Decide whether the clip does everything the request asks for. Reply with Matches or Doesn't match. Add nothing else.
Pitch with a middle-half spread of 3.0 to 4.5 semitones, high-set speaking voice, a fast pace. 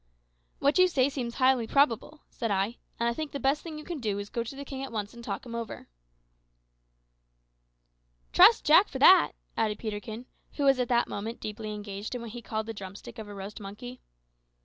Matches